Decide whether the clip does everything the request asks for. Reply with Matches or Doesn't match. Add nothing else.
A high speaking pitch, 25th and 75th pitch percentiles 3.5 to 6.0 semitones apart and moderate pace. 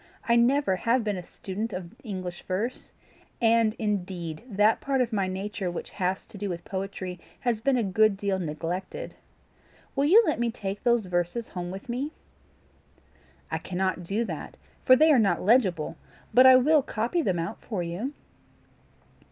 Matches